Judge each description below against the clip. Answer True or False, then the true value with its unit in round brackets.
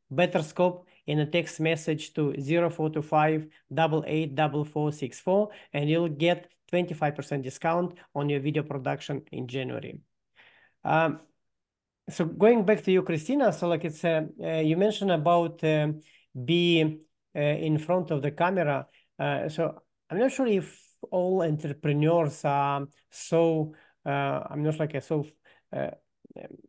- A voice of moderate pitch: True (160 Hz)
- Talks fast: False (155 wpm)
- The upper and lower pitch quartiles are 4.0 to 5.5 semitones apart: False (2.6 semitones)